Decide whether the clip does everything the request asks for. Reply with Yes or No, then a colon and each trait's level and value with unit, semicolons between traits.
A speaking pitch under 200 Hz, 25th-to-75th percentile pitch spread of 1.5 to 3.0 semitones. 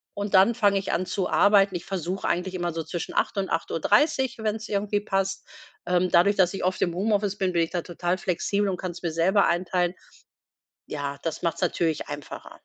Yes: medium, 185 Hz; narrow, 2.6 semitones